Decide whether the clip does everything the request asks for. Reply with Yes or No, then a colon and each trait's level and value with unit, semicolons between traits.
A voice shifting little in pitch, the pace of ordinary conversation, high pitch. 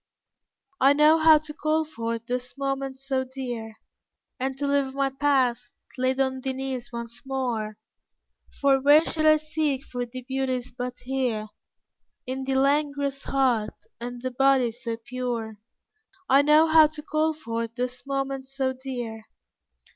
Yes: narrow, 2.3 semitones; average, 150 wpm; very high, 265 Hz